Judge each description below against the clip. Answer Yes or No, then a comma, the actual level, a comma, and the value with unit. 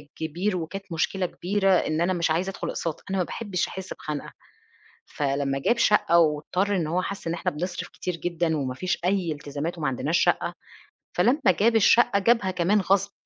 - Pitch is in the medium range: Yes, medium, 175 Hz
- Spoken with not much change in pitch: No, average, 3.6 semitones